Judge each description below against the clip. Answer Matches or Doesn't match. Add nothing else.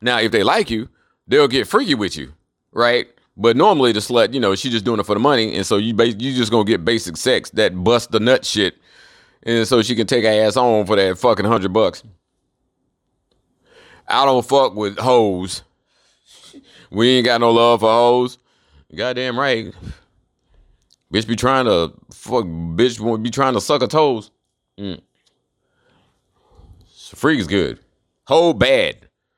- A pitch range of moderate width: Matches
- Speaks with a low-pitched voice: Matches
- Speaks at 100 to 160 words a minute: Doesn't match